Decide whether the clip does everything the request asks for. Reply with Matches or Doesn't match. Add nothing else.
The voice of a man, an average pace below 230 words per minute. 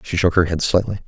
Doesn't match